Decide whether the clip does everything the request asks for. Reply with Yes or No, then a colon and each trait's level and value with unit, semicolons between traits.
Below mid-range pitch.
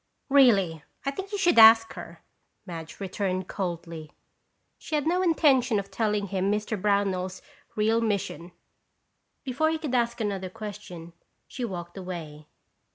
No: high, 205 Hz